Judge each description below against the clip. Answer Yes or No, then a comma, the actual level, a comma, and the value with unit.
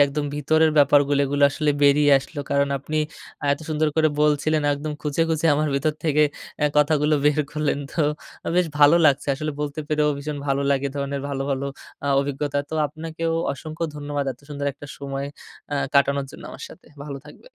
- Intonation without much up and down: Yes, narrow, 1.5 semitones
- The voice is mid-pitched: Yes, medium, 145 Hz